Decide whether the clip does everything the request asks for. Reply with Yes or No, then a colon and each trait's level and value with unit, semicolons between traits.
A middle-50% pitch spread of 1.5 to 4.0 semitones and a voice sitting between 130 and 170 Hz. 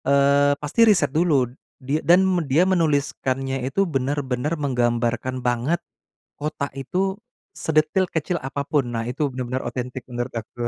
Yes: average, 3.4 semitones; medium, 140 Hz